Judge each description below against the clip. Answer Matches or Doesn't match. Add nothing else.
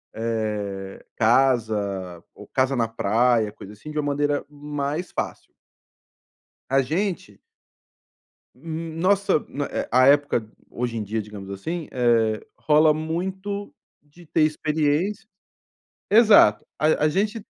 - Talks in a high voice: Doesn't match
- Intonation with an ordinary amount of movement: Doesn't match